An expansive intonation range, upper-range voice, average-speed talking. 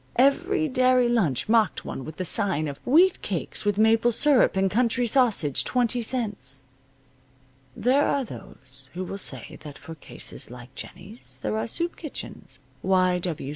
Yes: wide, 8.3 semitones; high, 215 Hz; average, 155 wpm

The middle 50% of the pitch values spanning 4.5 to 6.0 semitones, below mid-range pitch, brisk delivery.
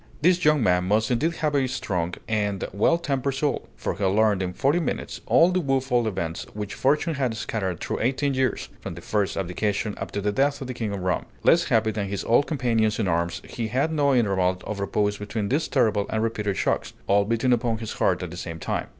Yes: average, 5.2 semitones; low, 110 Hz; fast, 225 wpm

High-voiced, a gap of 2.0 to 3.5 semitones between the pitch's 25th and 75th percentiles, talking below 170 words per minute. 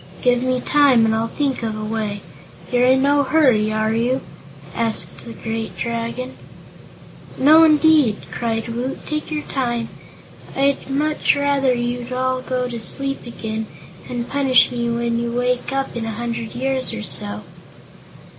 Yes: high, 245 Hz; average, 2.8 semitones; average, 155 wpm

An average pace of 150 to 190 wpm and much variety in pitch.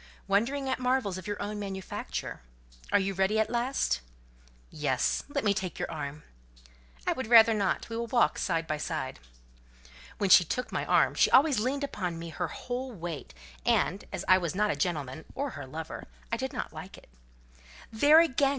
Yes: average, 185 wpm; wide, 6.8 semitones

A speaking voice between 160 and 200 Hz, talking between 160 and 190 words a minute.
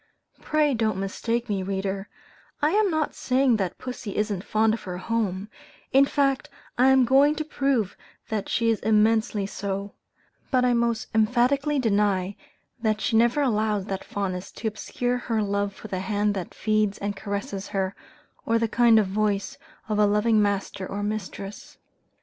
No: high, 215 Hz; average, 165 wpm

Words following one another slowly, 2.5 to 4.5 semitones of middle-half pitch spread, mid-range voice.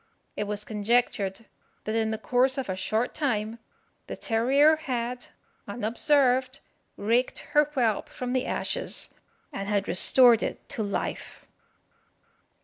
No: slow, 130 wpm; average, 3.4 semitones; high, 235 Hz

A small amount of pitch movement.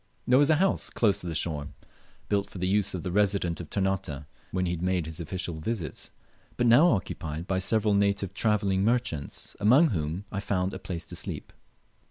No: average, 3.3 semitones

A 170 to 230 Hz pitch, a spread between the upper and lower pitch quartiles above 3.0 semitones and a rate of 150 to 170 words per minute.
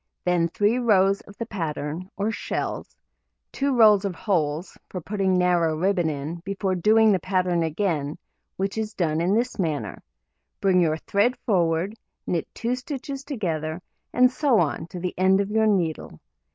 Yes: medium, 185 Hz; average, 4.3 semitones; average, 165 wpm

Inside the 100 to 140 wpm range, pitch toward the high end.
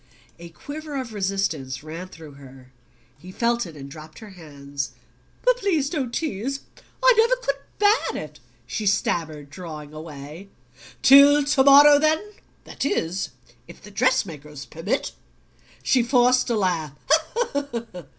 Yes: slow, 135 wpm; high, 195 Hz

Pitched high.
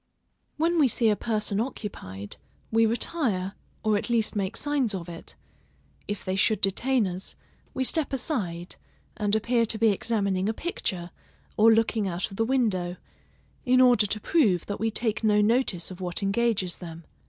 Yes: high, 215 Hz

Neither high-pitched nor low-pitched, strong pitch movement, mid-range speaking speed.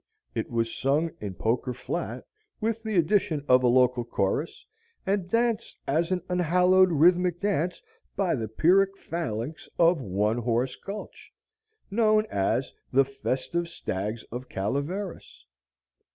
No: medium, 160 Hz; wide, 7.0 semitones; slow, 130 wpm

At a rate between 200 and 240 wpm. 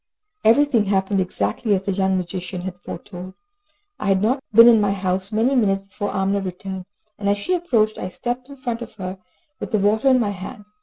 Yes: fast, 205 wpm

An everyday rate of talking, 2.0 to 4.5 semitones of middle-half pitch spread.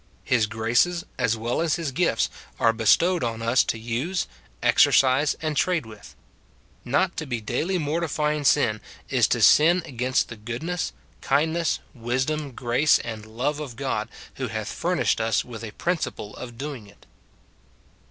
No: average, 150 wpm; average, 5.3 semitones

